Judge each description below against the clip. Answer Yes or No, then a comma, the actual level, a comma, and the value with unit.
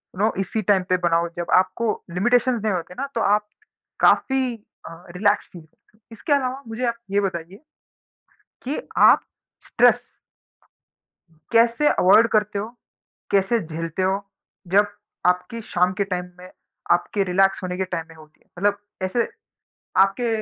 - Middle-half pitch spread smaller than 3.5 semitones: No, average, 4.1 semitones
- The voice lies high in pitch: Yes, high, 200 Hz